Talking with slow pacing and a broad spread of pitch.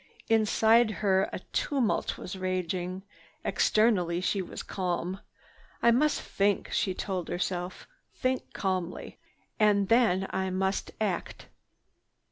No: slow, 110 wpm; average, 2.9 semitones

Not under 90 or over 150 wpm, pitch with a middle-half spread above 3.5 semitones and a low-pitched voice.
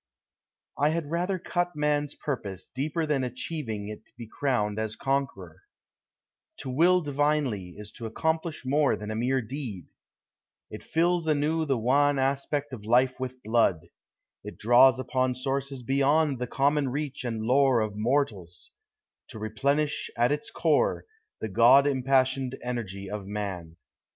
Yes: average, 145 wpm; average, 4.9 semitones; low, 130 Hz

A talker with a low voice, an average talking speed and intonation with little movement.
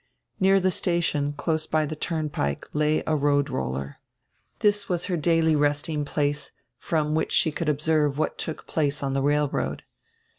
No: medium, 150 Hz; average, 160 wpm; narrow, 1.9 semitones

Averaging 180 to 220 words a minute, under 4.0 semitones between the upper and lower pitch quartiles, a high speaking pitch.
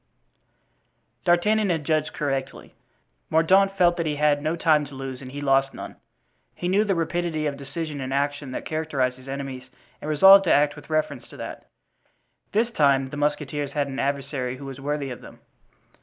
No: average, 185 wpm; average, 3.1 semitones; medium, 145 Hz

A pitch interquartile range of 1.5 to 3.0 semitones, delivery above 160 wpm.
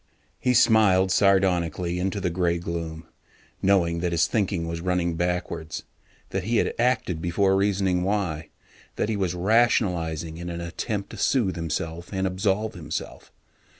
No: average, 2.7 semitones; average, 150 wpm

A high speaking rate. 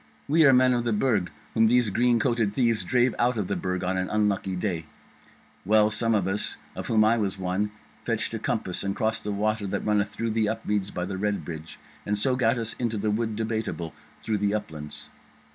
Yes: fast, 210 wpm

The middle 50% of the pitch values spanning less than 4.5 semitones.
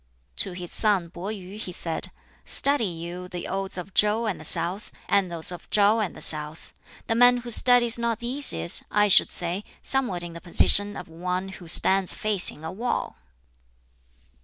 Yes: average, 3.9 semitones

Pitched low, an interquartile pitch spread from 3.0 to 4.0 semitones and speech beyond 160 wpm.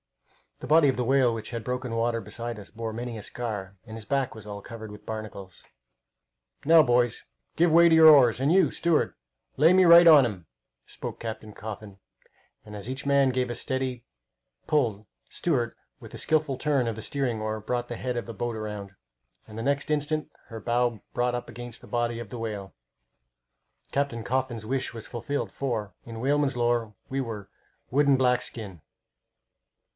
Yes: low, 120 Hz; average, 3.6 semitones; average, 190 wpm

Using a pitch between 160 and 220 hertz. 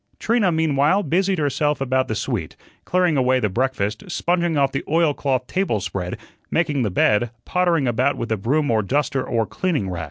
No: medium, 140 Hz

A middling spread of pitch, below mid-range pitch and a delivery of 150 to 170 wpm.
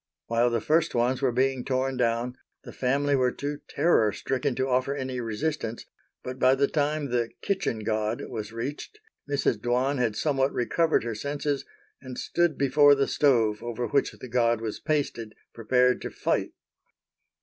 Yes: average, 3.2 semitones; low, 130 Hz; average, 165 wpm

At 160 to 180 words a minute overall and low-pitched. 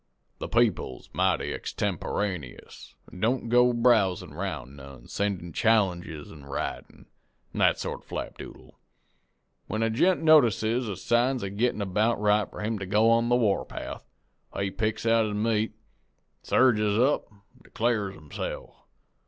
No: average, 145 wpm; low, 105 Hz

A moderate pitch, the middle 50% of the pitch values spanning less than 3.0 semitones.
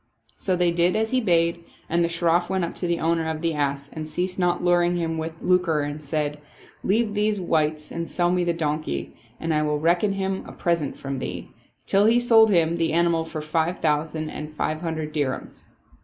Yes: medium, 170 Hz; narrow, 2.4 semitones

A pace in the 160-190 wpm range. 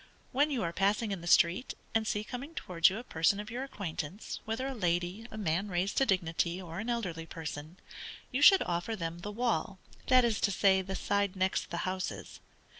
No: fast, 205 wpm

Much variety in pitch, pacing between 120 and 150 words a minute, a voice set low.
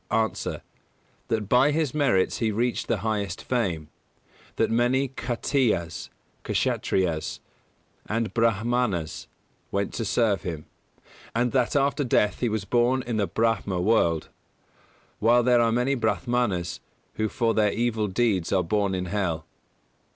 No: average, 4.0 semitones; slow, 135 wpm; low, 110 Hz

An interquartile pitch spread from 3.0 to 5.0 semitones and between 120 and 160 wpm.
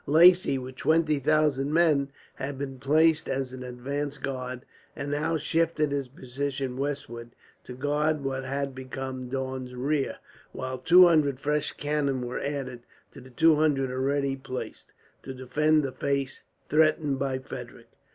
No: narrow, 2.5 semitones; average, 150 wpm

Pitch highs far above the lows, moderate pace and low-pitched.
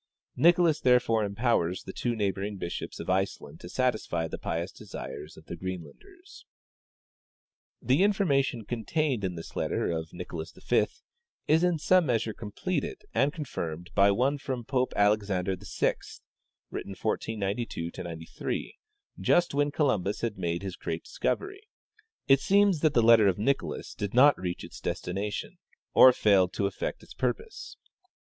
Yes: wide, 7.1 semitones; average, 145 wpm; low, 110 Hz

